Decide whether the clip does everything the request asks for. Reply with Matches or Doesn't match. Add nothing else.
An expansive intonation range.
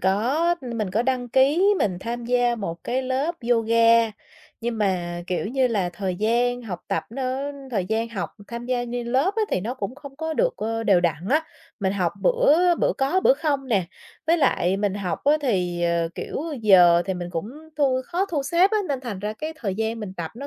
Matches